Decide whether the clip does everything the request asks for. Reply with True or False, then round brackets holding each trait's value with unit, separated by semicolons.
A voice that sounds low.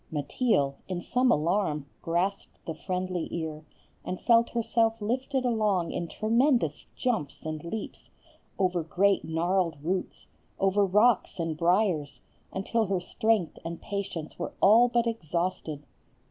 False (185 Hz)